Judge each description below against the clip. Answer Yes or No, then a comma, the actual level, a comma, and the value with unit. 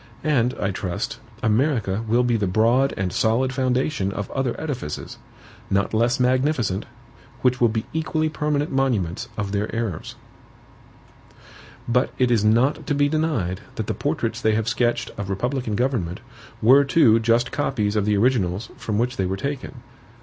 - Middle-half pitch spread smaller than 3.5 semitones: No, average, 4.4 semitones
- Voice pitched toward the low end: Yes, low, 120 Hz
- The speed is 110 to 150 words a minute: No, average, 160 wpm